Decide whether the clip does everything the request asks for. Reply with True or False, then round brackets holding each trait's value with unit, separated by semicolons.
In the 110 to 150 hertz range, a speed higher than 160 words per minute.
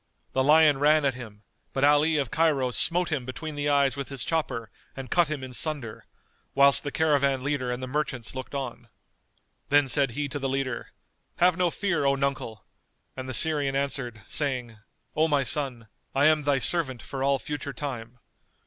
True (140 Hz; 185 wpm)